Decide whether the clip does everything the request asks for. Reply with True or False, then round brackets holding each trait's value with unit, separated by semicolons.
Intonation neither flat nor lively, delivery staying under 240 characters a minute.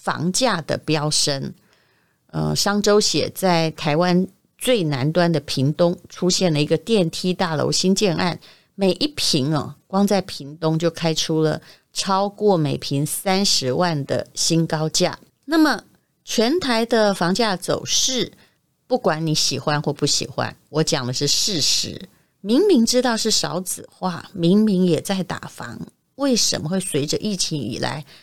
True (4.5 semitones; 215 characters per minute)